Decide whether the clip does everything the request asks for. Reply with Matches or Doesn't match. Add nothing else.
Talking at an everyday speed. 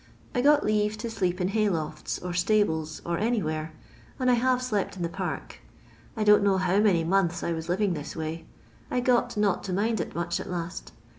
Doesn't match